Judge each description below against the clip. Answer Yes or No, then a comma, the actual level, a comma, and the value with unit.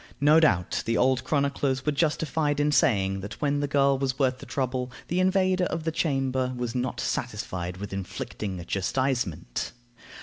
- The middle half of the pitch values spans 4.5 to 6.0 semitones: Yes, average, 4.8 semitones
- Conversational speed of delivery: Yes, average, 170 wpm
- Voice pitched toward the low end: Yes, low, 130 Hz